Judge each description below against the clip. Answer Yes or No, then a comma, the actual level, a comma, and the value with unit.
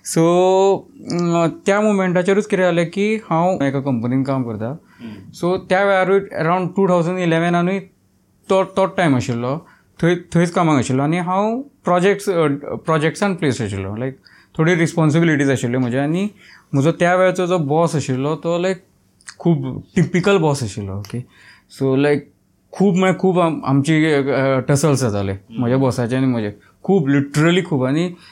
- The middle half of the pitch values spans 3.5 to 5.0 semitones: No, wide, 5.6 semitones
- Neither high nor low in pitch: Yes, medium, 160 Hz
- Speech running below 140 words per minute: Yes, average, 115 wpm